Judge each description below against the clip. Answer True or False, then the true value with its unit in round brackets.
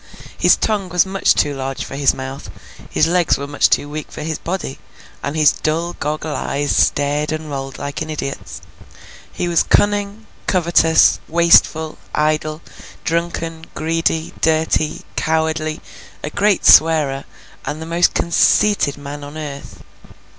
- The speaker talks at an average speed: True (145 wpm)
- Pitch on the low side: False (155 Hz)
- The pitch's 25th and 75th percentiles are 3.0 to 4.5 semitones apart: False (2.5 semitones)